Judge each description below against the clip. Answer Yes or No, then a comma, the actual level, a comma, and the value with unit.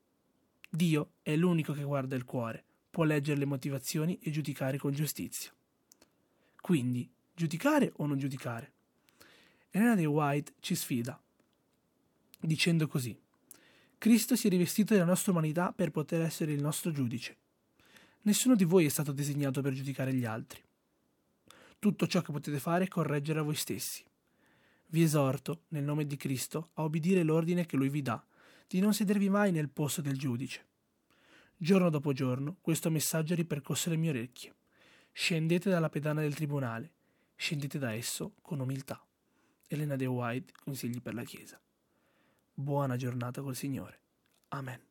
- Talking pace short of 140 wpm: No, average, 150 wpm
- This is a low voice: No, medium, 150 Hz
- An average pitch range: Yes, average, 4.0 semitones